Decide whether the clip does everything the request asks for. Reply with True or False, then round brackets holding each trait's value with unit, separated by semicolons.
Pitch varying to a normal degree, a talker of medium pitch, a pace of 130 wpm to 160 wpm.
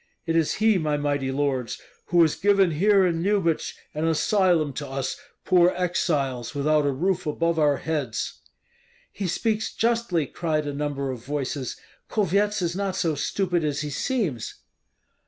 True (4.5 semitones; 160 Hz; 155 wpm)